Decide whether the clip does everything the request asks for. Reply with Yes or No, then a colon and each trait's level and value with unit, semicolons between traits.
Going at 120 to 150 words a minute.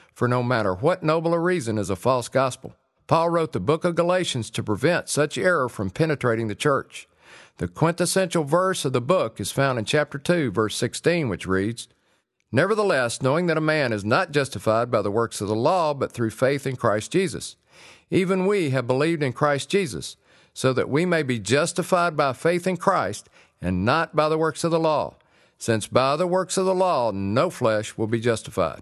No: average, 200 wpm